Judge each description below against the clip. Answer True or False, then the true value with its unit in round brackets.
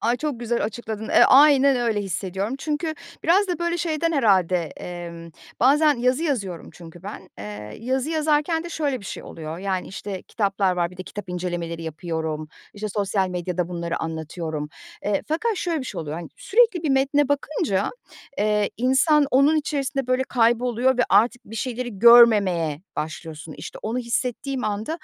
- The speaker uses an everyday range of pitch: False (7.6 semitones)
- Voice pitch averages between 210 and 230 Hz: True (225 Hz)